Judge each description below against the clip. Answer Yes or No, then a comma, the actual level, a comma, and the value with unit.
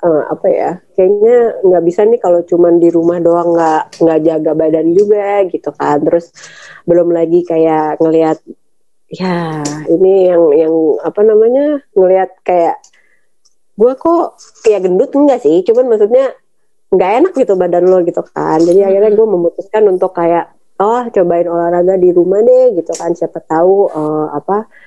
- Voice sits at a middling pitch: Yes, medium, 180 Hz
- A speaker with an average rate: No, fast, 160 wpm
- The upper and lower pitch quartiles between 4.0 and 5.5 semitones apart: Yes, average, 4.3 semitones